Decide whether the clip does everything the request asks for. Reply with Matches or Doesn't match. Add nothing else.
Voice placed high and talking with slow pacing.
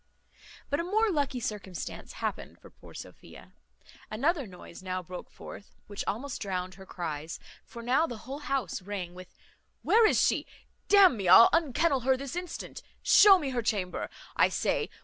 Doesn't match